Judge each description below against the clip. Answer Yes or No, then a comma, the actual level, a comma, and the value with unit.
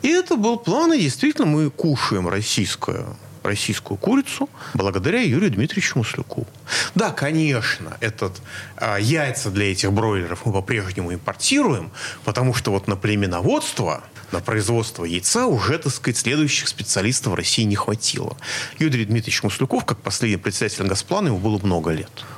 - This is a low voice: Yes, low, 115 Hz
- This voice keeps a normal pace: Yes, average, 145 wpm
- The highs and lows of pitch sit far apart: Yes, wide, 5.8 semitones